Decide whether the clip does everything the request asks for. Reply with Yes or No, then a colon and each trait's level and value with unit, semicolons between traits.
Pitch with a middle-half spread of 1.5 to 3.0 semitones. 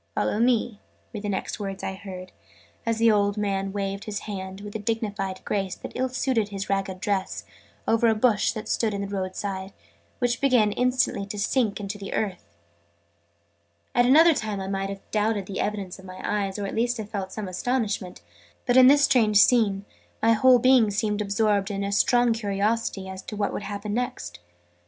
Yes: narrow, 2.6 semitones